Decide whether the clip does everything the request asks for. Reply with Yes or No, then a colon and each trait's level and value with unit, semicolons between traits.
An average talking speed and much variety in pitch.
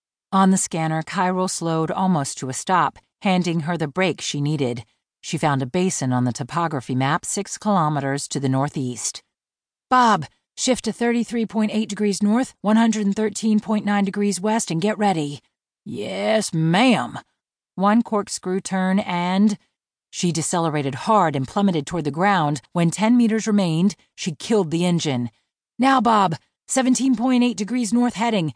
Yes: average, 145 wpm; wide, 5.7 semitones